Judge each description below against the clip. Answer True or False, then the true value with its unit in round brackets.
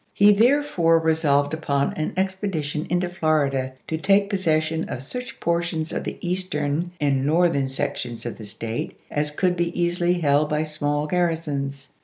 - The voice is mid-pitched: True (160 Hz)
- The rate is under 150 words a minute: False (160 wpm)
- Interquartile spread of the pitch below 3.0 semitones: False (3.6 semitones)